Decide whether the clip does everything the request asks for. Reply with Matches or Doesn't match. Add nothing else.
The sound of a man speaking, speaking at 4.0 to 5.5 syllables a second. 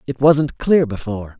Matches